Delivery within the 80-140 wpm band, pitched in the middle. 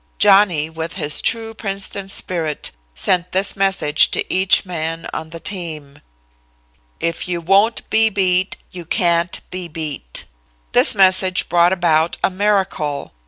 Yes: slow, 135 wpm; medium, 180 Hz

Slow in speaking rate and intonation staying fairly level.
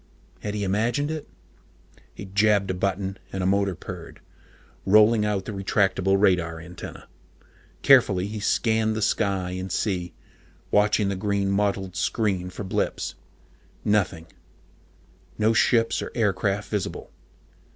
Yes: slow, 130 wpm; narrow, 2.1 semitones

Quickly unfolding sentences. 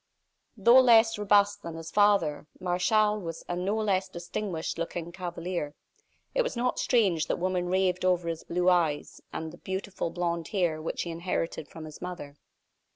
No: average, 165 wpm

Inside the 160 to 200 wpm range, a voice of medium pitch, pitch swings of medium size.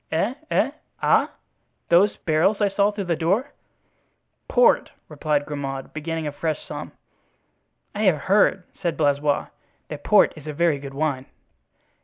No: average, 145 wpm; medium, 160 Hz; average, 4.9 semitones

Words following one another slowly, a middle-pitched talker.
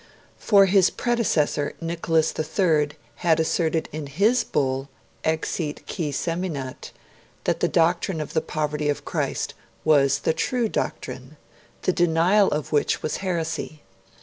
Yes: slow, 130 wpm; medium, 160 Hz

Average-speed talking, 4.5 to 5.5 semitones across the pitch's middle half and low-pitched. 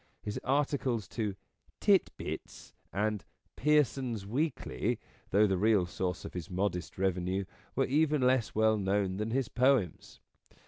Yes: average, 150 wpm; average, 5.2 semitones; low, 105 Hz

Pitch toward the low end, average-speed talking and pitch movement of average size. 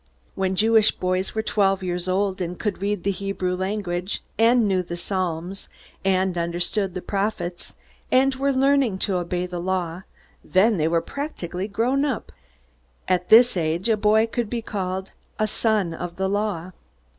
No: high, 190 Hz; average, 165 wpm; average, 3.3 semitones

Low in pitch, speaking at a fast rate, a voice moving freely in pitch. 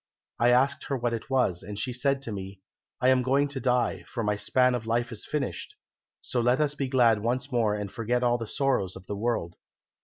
No: low, 120 Hz; fast, 225 wpm; average, 3.5 semitones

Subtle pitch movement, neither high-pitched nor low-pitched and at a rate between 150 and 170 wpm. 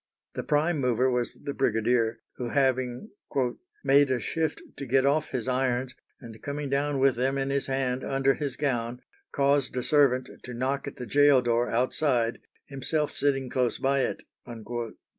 No: narrow, 2.2 semitones; low, 130 Hz; average, 165 wpm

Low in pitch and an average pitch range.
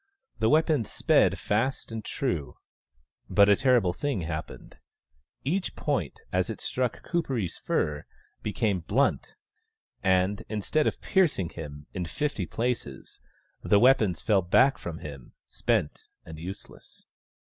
No: low, 105 Hz; wide, 7.2 semitones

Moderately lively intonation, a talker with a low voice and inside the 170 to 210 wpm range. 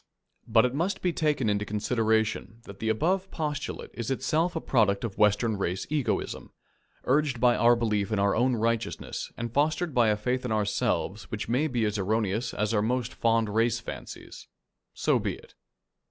Yes: average, 3.4 semitones; low, 115 Hz; average, 180 wpm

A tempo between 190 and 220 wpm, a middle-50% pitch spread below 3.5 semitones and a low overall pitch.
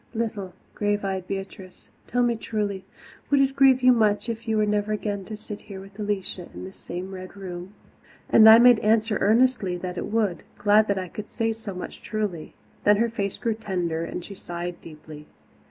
No: average, 200 wpm; average, 3.0 semitones; high, 205 Hz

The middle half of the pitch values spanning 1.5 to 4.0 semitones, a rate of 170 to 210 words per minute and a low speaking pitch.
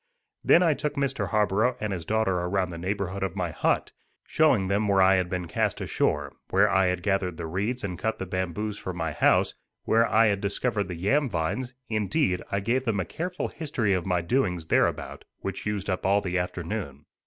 Yes: average, 3.6 semitones; fast, 205 wpm; low, 100 Hz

